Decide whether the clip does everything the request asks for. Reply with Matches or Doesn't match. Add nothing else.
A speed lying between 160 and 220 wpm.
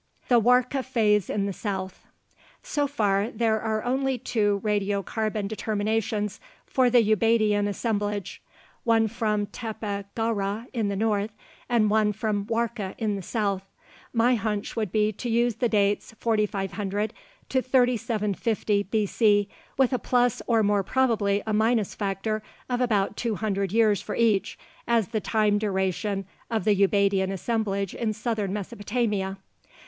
Doesn't match